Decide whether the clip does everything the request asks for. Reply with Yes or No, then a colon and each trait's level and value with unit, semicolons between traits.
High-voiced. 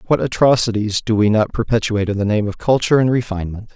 No: low, 110 Hz